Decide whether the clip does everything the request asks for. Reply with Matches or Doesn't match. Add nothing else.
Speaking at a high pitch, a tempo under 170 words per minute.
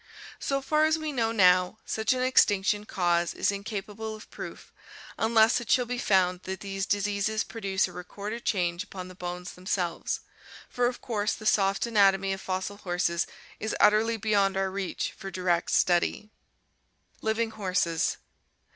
Matches